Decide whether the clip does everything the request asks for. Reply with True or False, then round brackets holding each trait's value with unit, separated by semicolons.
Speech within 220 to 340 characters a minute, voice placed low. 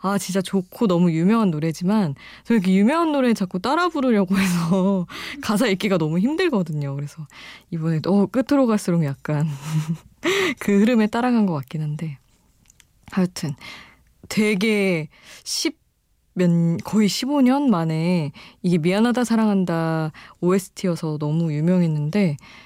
False (280 characters per minute; 185 Hz)